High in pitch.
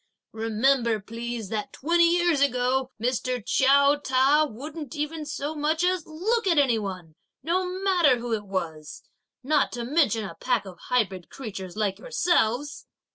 Yes: very high, 260 Hz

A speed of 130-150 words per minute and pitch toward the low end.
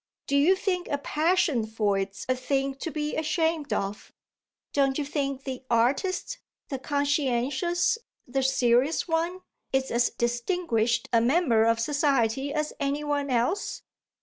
No: average, 145 wpm; very high, 275 Hz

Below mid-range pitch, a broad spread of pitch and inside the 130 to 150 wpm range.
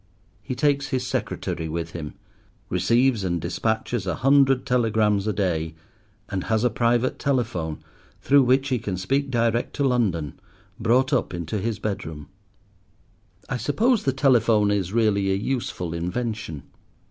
Yes: low, 110 Hz; wide, 5.7 semitones; average, 145 wpm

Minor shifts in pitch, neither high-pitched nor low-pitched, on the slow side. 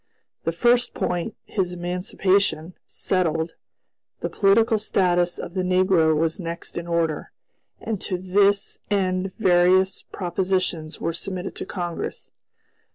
Yes: narrow, 2.1 semitones; medium, 180 Hz; slow, 120 wpm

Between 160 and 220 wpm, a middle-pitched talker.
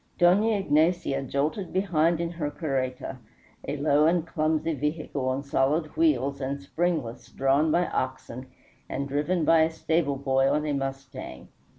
No: average, 150 wpm; medium, 150 Hz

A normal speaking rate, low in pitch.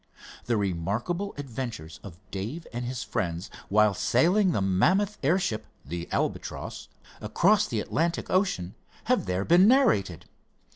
No: slow, 130 wpm; low, 120 Hz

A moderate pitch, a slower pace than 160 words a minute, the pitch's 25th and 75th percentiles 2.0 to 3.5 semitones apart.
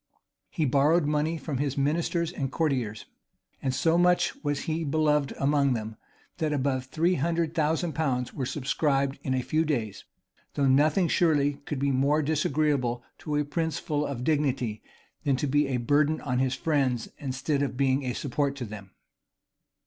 No: medium, 145 Hz; average, 170 wpm; average, 2.9 semitones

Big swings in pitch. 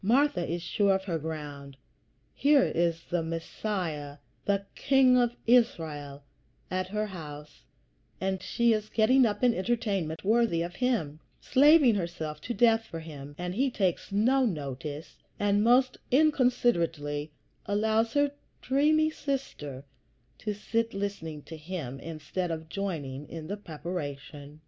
Yes: wide, 6.8 semitones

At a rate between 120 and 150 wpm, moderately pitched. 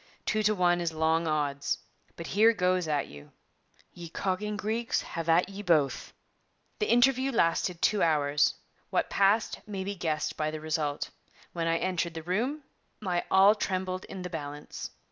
No: average, 165 wpm; medium, 175 Hz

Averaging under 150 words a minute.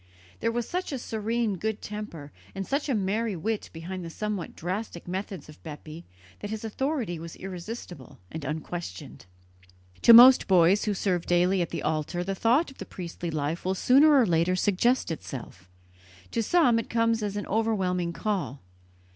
No: average, 170 wpm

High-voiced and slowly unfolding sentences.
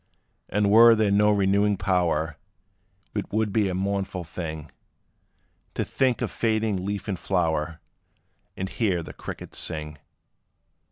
No: very low, 95 Hz; slow, 130 wpm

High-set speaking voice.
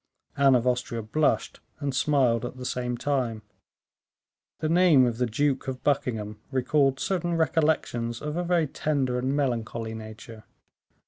No: low, 130 Hz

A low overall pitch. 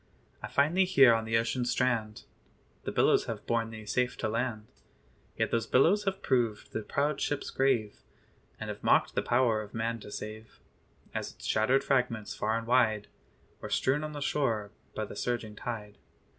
Yes: low, 115 Hz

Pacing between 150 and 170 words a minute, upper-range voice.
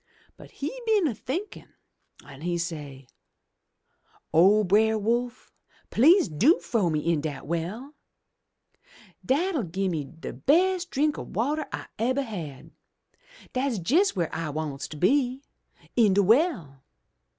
No: average, 140 wpm; high, 215 Hz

